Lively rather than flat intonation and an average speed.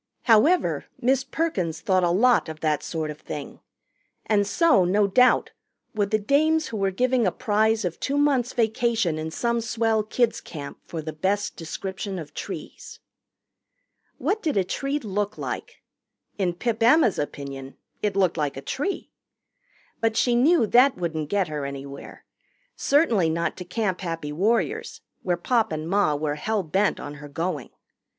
Yes: wide, 6.5 semitones; average, 165 wpm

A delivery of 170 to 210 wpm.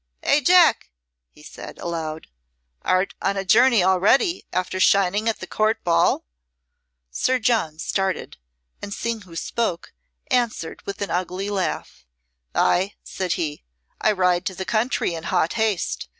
No: average, 145 wpm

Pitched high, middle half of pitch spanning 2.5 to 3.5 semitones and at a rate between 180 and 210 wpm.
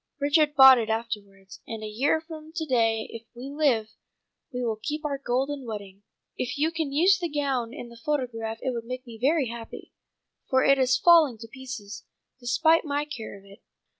No: very high, 255 Hz; average, 4.4 semitones; average, 195 wpm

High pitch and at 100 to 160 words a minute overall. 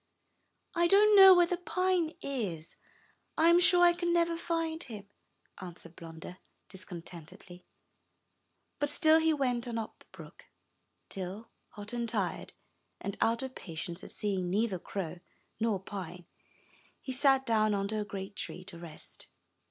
Yes: high, 220 Hz; average, 150 wpm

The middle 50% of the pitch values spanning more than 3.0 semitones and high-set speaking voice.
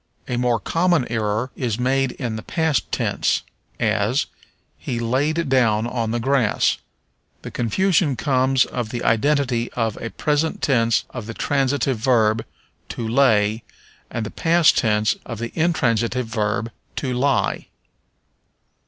No: average, 3.4 semitones; low, 125 Hz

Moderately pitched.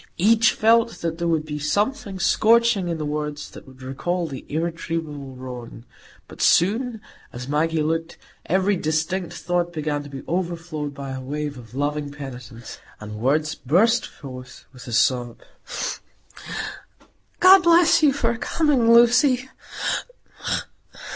Yes: medium, 160 Hz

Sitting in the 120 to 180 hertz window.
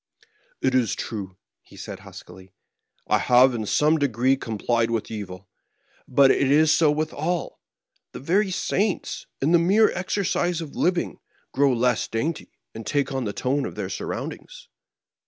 Yes: low, 135 Hz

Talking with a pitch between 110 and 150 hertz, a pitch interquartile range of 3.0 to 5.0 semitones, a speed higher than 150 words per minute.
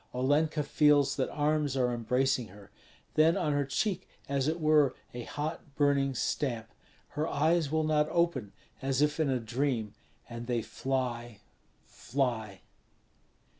No: medium, 140 Hz; average, 3.7 semitones; average, 140 wpm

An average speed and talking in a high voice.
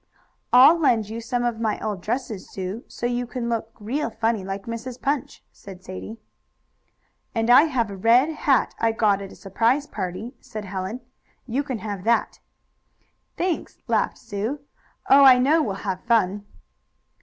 Yes: average, 165 wpm; high, 230 Hz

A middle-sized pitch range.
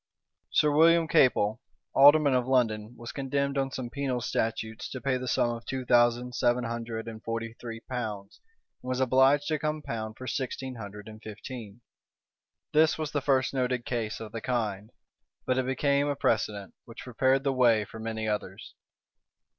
Yes: average, 3.1 semitones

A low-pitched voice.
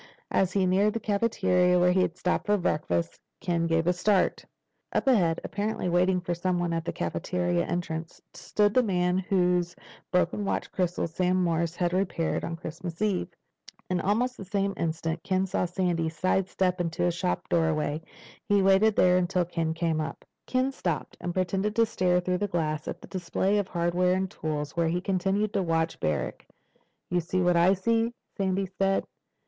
No: medium, 180 Hz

